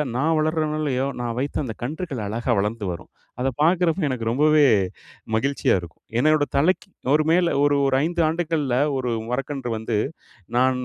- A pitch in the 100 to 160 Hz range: Yes, medium, 140 Hz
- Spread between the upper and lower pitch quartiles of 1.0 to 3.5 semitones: No, average, 4.2 semitones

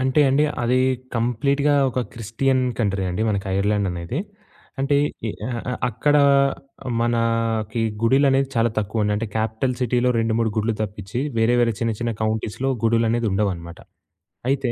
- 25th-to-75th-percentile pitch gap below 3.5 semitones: Yes, average, 2.9 semitones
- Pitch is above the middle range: No, low, 115 Hz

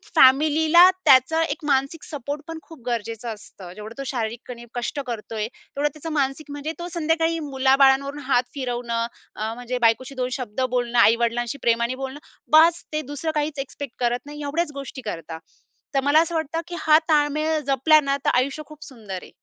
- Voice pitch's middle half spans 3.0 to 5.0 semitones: Yes, average, 4.2 semitones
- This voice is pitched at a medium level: No, very high, 270 Hz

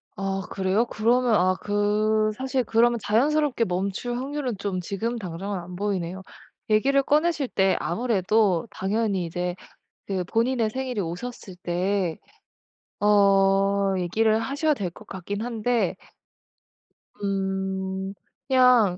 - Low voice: No, high, 205 Hz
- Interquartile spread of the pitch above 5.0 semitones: No, average, 3.9 semitones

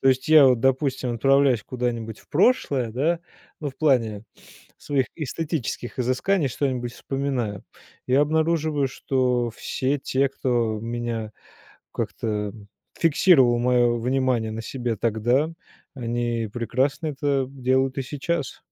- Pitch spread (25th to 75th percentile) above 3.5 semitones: No, average, 2.9 semitones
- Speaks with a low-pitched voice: Yes, low, 130 Hz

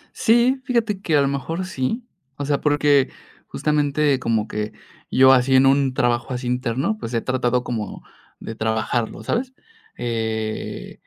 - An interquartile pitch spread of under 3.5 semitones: No, average, 4.1 semitones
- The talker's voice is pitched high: No, low, 130 Hz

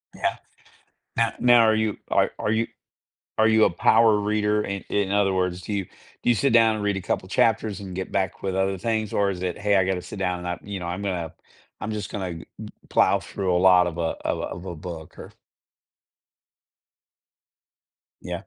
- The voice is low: Yes, low, 100 Hz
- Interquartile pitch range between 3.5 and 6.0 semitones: No, average, 2.8 semitones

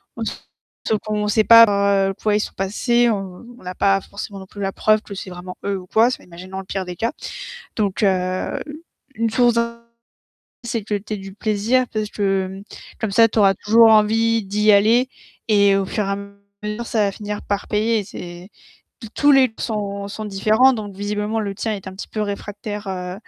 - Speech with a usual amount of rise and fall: No, narrow, 2.2 semitones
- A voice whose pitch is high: Yes, high, 210 Hz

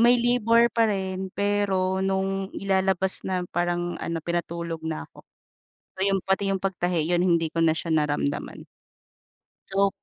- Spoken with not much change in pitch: Yes, narrow, 2.3 semitones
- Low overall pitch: No, high, 190 Hz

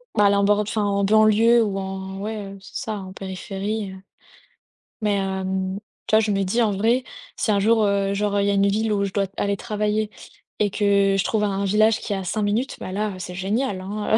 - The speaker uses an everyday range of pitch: No, narrow, 1.6 semitones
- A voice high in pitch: Yes, high, 200 Hz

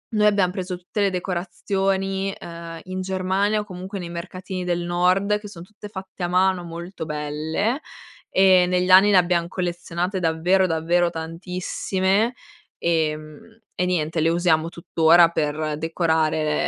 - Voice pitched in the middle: Yes, medium, 180 Hz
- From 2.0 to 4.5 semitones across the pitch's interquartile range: Yes, narrow, 2.3 semitones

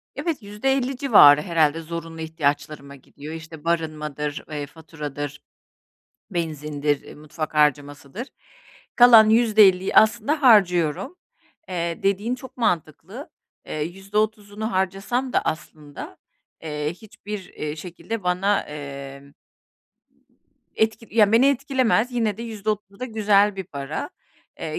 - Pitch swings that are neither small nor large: No, wide, 6.4 semitones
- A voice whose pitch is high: No, medium, 180 Hz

